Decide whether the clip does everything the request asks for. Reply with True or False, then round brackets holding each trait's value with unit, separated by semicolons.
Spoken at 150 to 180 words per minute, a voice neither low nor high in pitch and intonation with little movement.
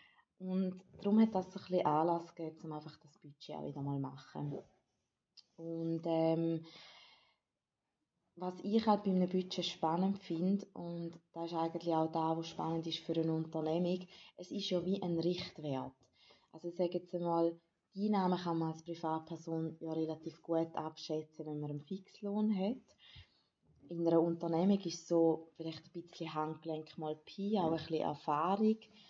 True (155 wpm; 165 Hz; 2.2 semitones)